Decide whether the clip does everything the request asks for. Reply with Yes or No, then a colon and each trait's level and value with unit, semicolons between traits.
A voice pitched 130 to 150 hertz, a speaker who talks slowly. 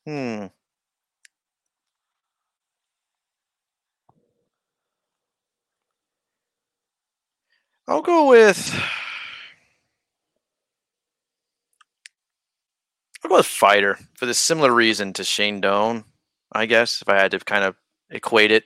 No: low, 110 Hz; slow, 80 wpm